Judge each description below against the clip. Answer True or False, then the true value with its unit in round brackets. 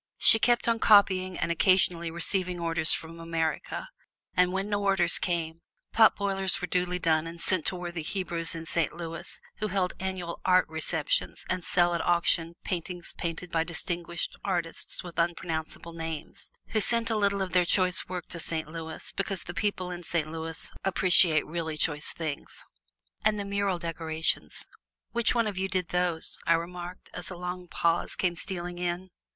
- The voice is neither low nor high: True (175 Hz)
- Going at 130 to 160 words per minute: False (170 wpm)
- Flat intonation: True (2.0 semitones)